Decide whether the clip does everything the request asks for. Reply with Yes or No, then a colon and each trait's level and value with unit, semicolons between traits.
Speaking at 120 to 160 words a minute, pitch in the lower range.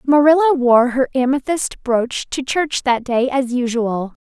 No: average, 155 wpm; very high, 260 Hz